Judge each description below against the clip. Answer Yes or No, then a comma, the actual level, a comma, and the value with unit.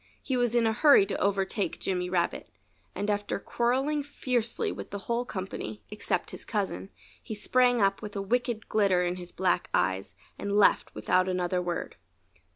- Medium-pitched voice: No, high, 200 Hz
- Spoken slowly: No, average, 170 wpm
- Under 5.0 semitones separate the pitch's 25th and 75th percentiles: Yes, average, 4.6 semitones